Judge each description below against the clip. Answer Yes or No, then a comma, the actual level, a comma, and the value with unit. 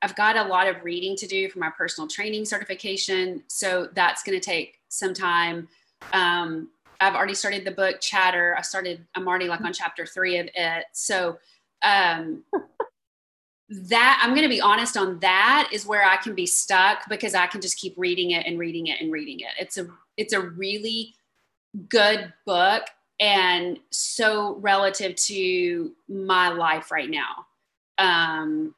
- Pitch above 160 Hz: Yes, high, 190 Hz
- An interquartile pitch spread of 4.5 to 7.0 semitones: No, average, 3.2 semitones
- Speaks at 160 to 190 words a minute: Yes, average, 170 wpm